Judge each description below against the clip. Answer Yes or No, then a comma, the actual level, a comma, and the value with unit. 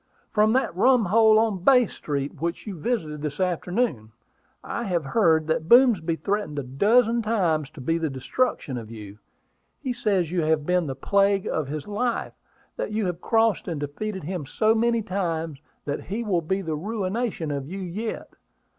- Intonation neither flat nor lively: No, wide, 6.1 semitones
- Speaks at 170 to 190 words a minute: Yes, average, 175 wpm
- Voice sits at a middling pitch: Yes, medium, 180 Hz